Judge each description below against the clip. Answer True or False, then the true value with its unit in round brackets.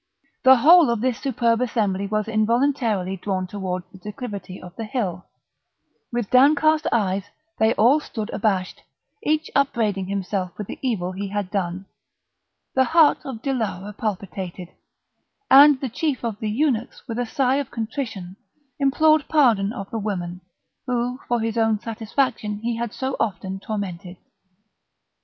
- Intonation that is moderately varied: True (4.7 semitones)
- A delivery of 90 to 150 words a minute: True (145 wpm)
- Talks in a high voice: True (220 Hz)